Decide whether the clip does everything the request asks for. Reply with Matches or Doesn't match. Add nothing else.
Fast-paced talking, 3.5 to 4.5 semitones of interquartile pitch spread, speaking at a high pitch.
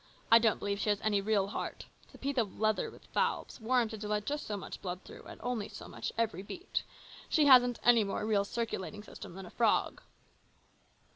Doesn't match